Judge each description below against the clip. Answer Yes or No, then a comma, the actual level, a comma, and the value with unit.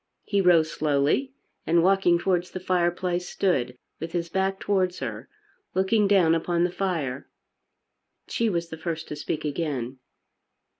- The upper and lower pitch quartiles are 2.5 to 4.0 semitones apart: Yes, average, 2.9 semitones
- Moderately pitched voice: Yes, medium, 175 Hz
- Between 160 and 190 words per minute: No, average, 145 wpm